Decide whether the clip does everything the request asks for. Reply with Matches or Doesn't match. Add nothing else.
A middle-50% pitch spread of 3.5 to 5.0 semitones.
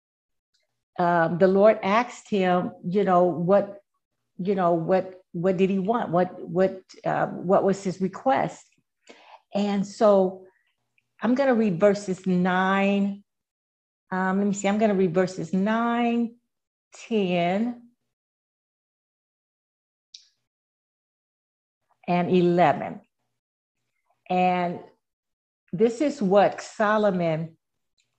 Doesn't match